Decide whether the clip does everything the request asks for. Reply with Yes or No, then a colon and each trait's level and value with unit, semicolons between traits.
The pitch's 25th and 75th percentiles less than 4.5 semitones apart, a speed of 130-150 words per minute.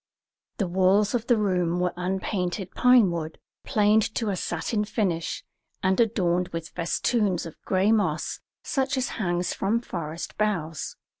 Yes: average, 3.6 semitones; average, 145 wpm